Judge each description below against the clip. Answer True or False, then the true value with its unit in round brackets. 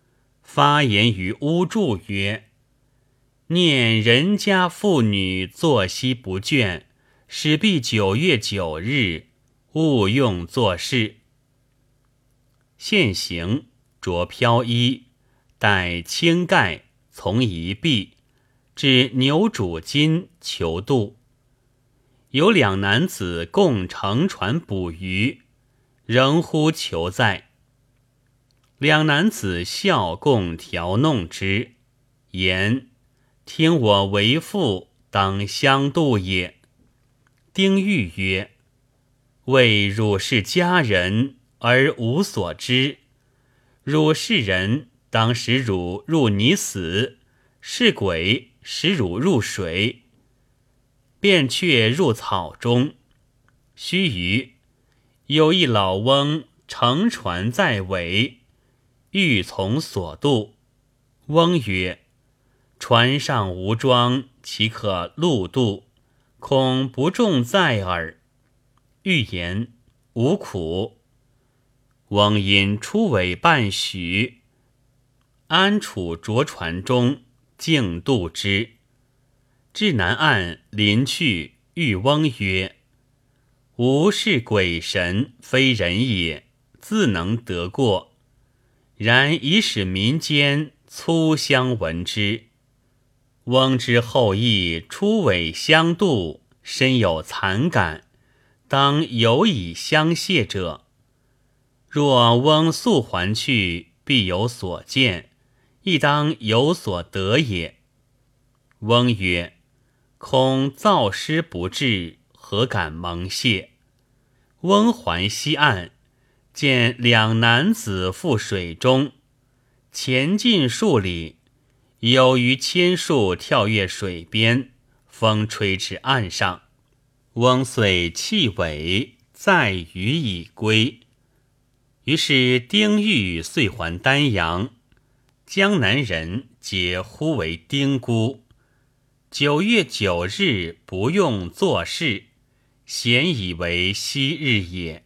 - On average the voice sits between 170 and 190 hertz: False (125 Hz)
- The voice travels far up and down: False (4.1 semitones)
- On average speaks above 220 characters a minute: False (120 characters per minute)